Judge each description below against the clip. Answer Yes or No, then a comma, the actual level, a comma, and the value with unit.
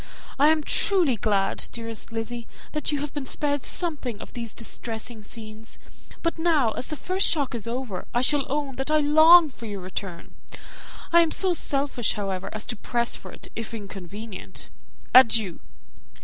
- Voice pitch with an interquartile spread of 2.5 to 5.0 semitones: No, wide, 5.4 semitones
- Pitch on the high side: Yes, high, 240 Hz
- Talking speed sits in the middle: Yes, average, 175 wpm